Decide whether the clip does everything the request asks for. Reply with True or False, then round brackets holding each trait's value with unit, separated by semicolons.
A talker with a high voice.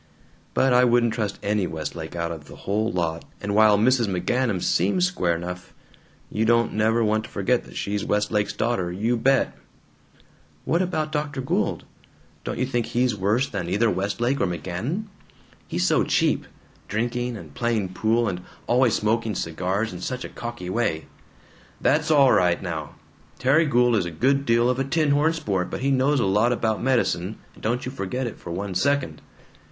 False (115 Hz)